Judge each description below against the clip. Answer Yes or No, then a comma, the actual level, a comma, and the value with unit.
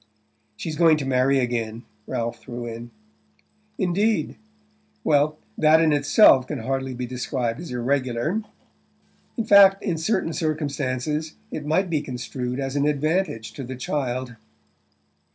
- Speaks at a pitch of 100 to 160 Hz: Yes, medium, 140 Hz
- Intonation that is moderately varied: Yes, average, 4.2 semitones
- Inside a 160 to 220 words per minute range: No, slow, 135 wpm